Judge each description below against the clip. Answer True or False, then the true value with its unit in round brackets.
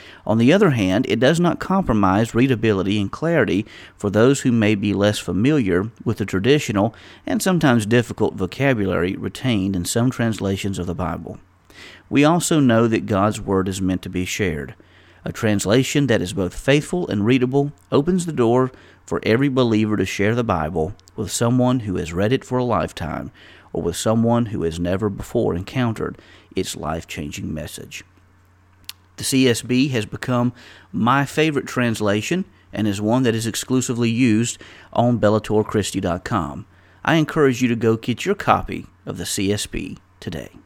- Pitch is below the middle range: True (110 Hz)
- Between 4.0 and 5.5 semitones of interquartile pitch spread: True (4.9 semitones)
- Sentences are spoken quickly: False (160 wpm)